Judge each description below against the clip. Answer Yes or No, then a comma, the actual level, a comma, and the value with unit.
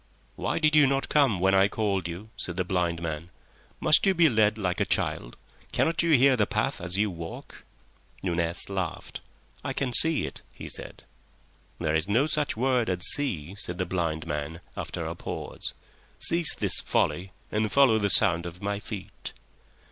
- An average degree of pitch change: No, wide, 7.0 semitones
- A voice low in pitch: Yes, low, 100 Hz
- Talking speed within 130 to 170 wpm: No, average, 180 wpm